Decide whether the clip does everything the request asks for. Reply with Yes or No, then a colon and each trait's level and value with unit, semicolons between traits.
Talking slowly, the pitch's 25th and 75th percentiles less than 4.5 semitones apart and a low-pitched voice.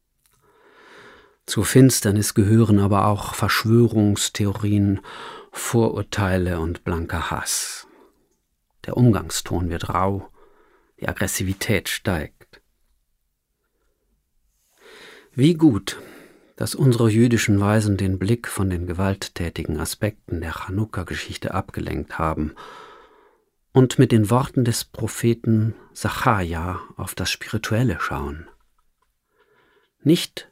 No: slow, 90 wpm; wide, 5.5 semitones; low, 105 Hz